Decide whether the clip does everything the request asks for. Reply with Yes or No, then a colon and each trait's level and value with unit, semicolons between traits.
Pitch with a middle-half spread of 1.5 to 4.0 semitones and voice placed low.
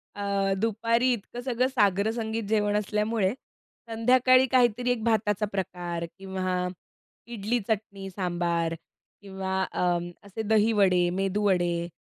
No: average, 3.3 semitones; high, 205 Hz